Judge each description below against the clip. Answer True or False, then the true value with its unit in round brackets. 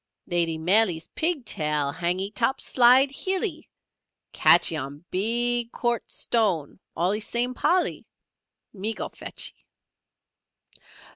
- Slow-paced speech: True (100 wpm)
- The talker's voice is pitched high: True (215 Hz)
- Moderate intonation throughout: False (6.0 semitones)